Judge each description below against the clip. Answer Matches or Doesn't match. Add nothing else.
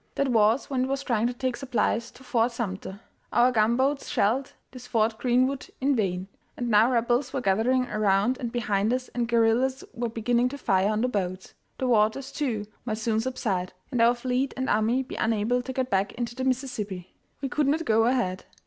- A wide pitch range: Doesn't match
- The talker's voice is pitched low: Doesn't match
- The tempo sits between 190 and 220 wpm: Matches